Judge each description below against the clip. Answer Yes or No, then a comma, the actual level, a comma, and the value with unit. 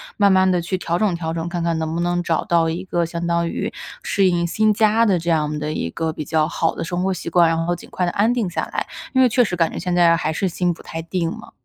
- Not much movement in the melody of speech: Yes, narrow, 2.1 semitones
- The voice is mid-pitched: Yes, medium, 170 Hz